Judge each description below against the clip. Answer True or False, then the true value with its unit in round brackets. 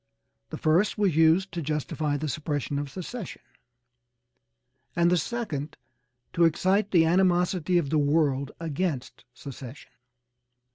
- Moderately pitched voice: True (160 Hz)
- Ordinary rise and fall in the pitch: True (3.7 semitones)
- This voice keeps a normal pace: False (125 wpm)